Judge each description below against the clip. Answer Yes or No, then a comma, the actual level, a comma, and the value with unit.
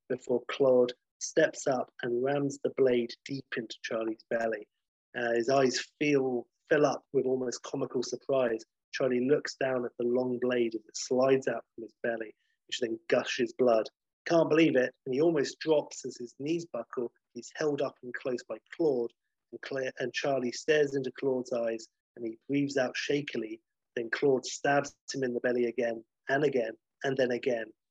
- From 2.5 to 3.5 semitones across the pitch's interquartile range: Yes, average, 2.8 semitones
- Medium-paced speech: Yes, average, 180 wpm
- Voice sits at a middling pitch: No, low, 130 Hz